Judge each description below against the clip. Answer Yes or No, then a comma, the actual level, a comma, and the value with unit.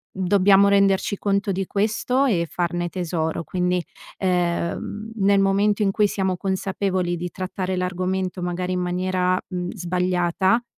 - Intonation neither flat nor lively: No, narrow, 1.7 semitones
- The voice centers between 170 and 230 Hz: Yes, medium, 185 Hz